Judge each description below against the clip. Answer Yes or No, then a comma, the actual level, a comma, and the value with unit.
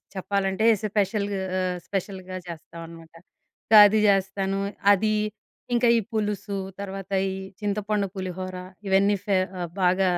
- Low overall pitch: No, high, 195 Hz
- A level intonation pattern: Yes, narrow, 1.8 semitones